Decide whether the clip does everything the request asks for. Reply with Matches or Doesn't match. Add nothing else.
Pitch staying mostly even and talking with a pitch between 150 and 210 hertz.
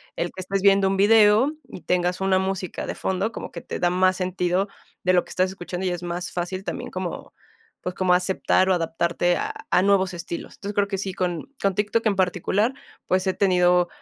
Matches